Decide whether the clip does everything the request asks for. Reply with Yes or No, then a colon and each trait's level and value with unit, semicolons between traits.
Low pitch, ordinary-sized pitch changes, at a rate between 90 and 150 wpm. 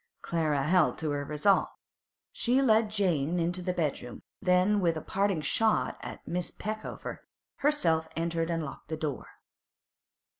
No: medium, 170 Hz; average, 4.2 semitones; average, 145 wpm